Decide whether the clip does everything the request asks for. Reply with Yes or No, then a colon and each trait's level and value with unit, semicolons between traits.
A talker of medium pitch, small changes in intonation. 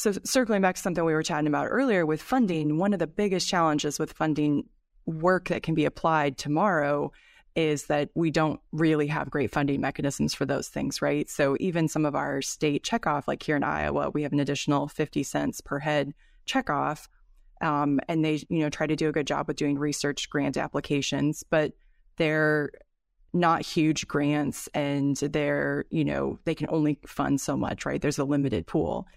Yes: medium, 150 Hz; narrow, 2.2 semitones